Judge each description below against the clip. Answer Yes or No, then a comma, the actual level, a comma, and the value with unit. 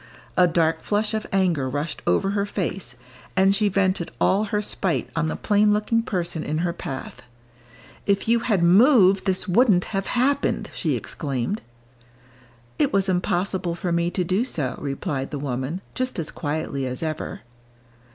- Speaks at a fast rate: No, average, 160 wpm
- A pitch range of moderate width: Yes, average, 4.4 semitones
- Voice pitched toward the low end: No, medium, 185 Hz